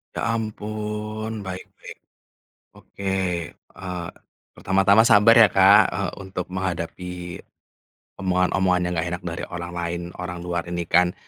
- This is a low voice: Yes, very low, 95 Hz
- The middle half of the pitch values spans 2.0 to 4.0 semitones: Yes, narrow, 2.6 semitones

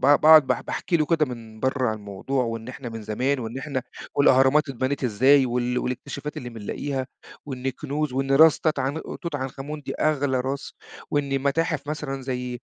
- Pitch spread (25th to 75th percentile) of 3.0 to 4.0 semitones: No, narrow, 2.6 semitones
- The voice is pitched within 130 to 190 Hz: Yes, low, 135 Hz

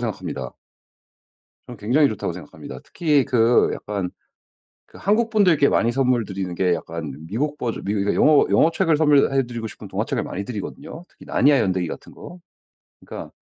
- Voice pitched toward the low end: Yes, low, 125 Hz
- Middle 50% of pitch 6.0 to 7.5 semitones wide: Yes, wide, 6.8 semitones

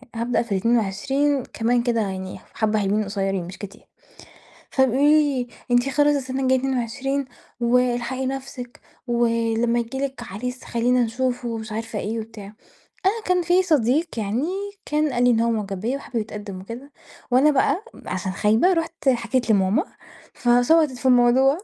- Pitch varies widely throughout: No, average, 3.3 semitones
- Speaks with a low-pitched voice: No, high, 245 Hz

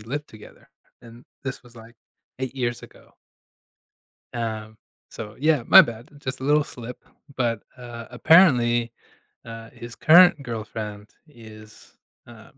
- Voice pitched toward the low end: Yes, low, 120 Hz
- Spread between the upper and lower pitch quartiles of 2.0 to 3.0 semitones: Yes, narrow, 2.6 semitones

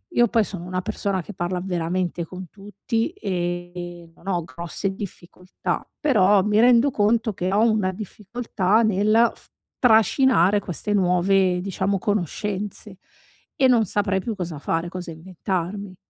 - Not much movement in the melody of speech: No, average, 3.1 semitones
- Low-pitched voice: No, high, 195 Hz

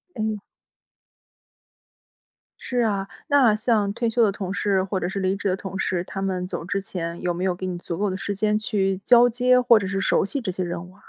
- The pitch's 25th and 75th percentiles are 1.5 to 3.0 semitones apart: Yes, average, 2.7 semitones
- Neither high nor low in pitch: No, high, 195 Hz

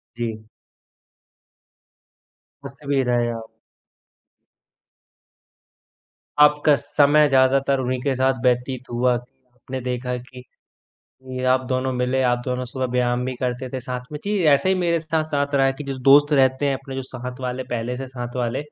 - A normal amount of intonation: No, narrow, 1.7 semitones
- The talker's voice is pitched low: Yes, low, 130 Hz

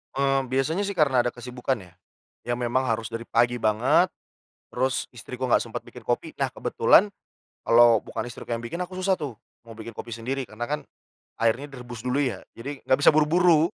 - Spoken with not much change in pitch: No, average, 3.3 semitones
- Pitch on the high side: No, low, 125 Hz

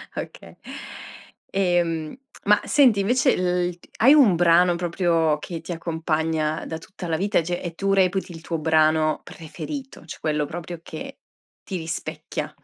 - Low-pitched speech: No, medium, 175 Hz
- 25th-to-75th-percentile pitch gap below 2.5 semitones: No, average, 2.8 semitones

